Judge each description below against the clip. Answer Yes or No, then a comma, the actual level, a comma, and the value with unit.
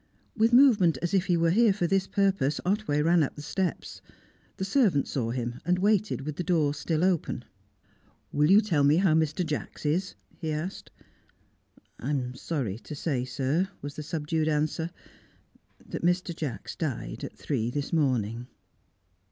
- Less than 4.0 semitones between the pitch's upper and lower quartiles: No, average, 4.3 semitones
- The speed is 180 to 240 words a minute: No, average, 170 wpm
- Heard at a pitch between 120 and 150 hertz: No, medium, 160 Hz